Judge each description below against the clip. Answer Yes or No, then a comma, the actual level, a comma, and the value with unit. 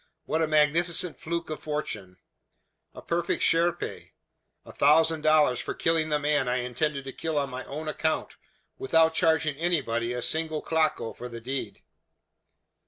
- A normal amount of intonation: Yes, average, 3.3 semitones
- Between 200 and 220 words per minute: No, average, 155 wpm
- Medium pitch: Yes, medium, 155 Hz